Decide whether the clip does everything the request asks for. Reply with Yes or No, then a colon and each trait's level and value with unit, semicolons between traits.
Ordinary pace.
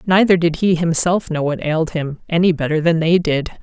No: fast, 215 wpm